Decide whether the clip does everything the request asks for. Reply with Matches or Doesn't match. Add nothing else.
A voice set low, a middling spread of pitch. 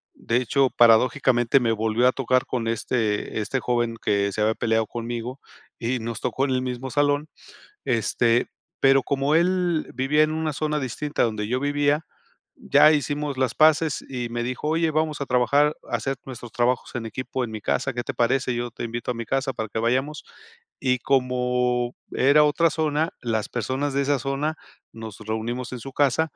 Matches